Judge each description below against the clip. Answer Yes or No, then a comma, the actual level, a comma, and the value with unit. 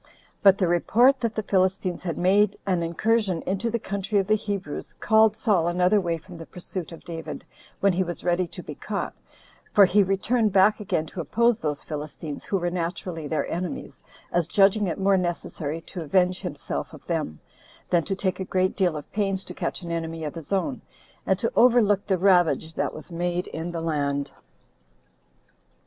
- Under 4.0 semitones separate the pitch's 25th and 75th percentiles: Yes, average, 3.2 semitones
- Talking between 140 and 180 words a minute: No, average, 195 wpm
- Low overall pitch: No, medium, 185 Hz